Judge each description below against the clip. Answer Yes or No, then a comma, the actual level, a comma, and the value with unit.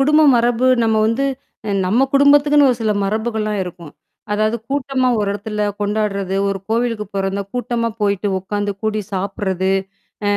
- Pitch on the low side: No, high, 215 Hz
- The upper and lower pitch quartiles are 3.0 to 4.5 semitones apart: Yes, average, 3.4 semitones